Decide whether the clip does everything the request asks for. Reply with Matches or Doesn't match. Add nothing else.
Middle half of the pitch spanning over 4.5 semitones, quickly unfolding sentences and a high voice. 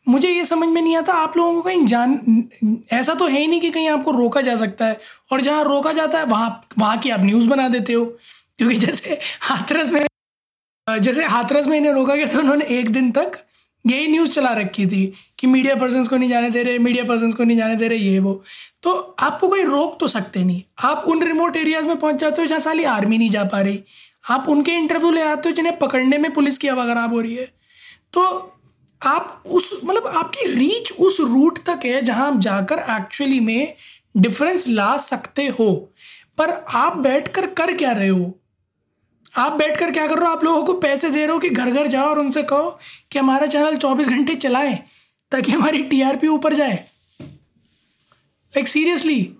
Matches